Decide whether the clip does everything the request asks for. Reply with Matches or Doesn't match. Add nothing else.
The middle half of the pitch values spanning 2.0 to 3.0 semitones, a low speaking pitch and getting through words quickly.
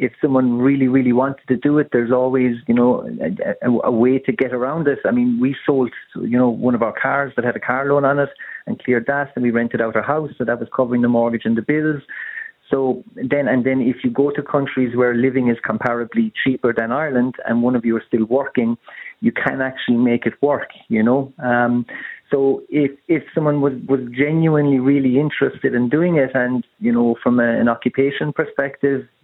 Matches